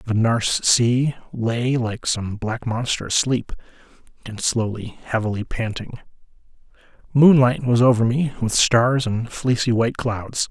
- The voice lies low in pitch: Yes, low, 120 Hz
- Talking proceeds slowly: Yes, slow, 130 wpm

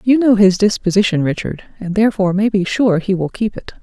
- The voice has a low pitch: No, high, 200 Hz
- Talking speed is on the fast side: Yes, fast, 220 wpm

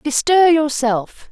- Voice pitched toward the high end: Yes, very high, 285 Hz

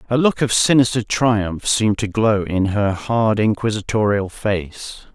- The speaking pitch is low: Yes, low, 105 Hz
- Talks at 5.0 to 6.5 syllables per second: No, 4.1 syllables/s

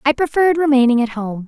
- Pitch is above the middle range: Yes, very high, 265 Hz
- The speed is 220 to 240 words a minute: No, fast, 205 wpm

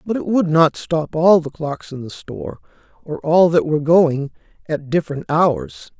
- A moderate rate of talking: Yes, average, 170 wpm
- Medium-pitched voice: Yes, medium, 160 Hz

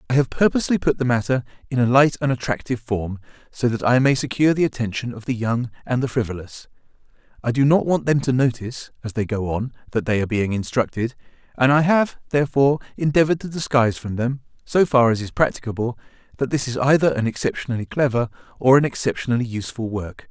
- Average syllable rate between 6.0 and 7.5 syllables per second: Yes, 6.5 syllables/s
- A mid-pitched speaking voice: No, low, 125 Hz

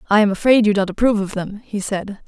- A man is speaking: No, female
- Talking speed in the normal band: No, fast, 265 wpm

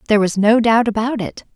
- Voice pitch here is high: Yes, high, 220 Hz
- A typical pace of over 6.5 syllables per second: No, 6.1 syllables/s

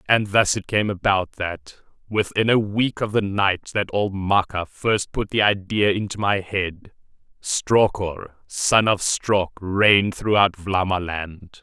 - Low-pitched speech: Yes, low, 100 Hz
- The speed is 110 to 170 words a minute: Yes, average, 150 wpm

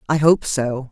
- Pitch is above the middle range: No, medium, 140 Hz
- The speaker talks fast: No, average, 195 wpm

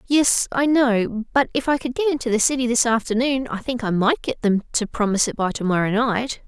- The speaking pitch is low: No, high, 240 Hz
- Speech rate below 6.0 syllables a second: Yes, 5.5 syllables/s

